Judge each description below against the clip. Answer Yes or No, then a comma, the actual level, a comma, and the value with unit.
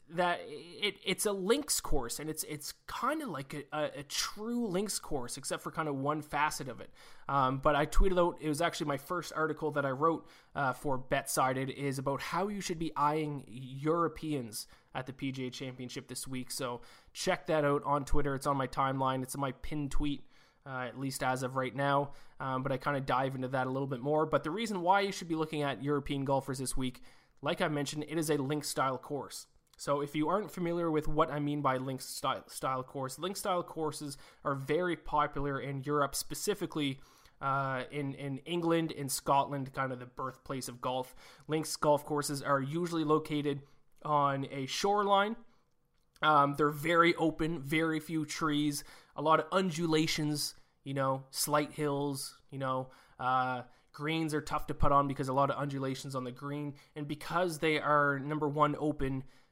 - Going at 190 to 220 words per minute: Yes, average, 200 wpm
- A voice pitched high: No, medium, 145 Hz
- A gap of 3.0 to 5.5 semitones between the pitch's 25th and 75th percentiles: No, narrow, 2.6 semitones